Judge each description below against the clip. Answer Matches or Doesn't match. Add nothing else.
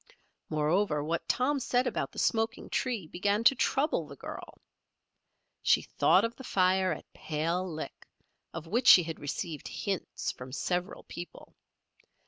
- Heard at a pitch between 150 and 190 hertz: Matches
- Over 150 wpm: Doesn't match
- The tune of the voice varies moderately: Doesn't match